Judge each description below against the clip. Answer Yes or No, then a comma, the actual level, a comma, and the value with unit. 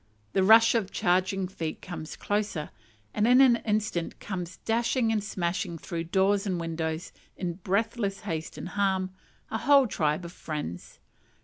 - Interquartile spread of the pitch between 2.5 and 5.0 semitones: Yes, average, 3.9 semitones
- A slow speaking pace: No, average, 150 wpm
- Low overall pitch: No, high, 190 Hz